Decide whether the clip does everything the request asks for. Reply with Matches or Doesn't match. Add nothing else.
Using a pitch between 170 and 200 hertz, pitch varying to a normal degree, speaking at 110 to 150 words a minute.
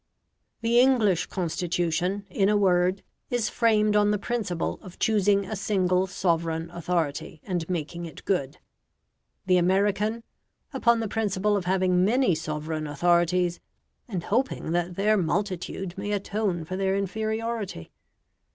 Matches